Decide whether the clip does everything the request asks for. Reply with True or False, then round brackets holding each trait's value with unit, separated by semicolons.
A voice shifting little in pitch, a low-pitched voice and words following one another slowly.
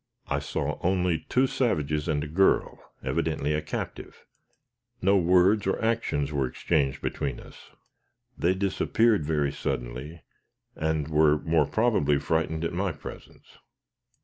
False (4.2 semitones; 80 Hz; 130 wpm)